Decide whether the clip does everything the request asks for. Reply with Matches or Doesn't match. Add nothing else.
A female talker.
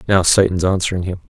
Doesn't match